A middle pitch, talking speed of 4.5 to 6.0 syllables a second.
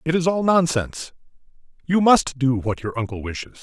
Yes: medium, 145 Hz; 5.3 syllables/s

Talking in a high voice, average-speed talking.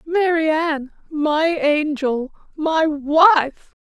No: very high, 310 Hz; slow, 95 wpm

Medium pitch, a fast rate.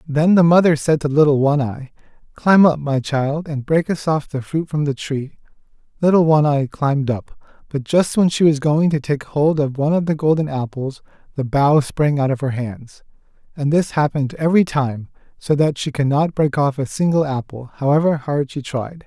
Yes: medium, 145 Hz; fast, 210 wpm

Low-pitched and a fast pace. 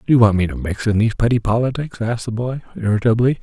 Yes: low, 115 Hz; fast, 245 wpm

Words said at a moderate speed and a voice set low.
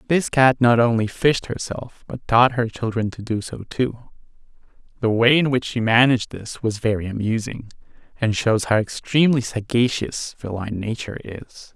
Yes: average, 165 wpm; low, 115 Hz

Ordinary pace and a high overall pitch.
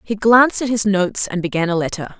No: fast, 245 wpm; high, 200 Hz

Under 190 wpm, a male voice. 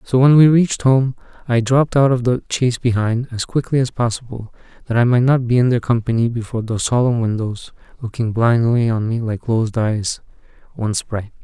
No: average, 195 wpm; male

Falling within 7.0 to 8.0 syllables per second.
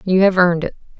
Yes: 7.4 syllables/s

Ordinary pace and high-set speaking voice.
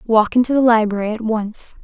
Yes: average, 195 wpm; high, 225 Hz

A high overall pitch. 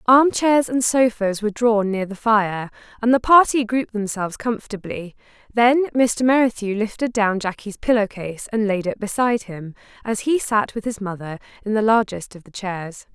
Yes: high, 215 Hz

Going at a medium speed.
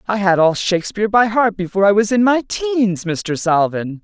No: fast, 210 wpm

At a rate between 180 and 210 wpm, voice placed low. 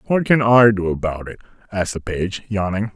Yes: fast, 205 wpm; low, 100 Hz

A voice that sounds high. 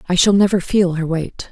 No: medium, 180 Hz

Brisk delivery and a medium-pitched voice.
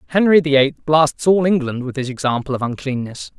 No: average, 195 wpm; medium, 145 Hz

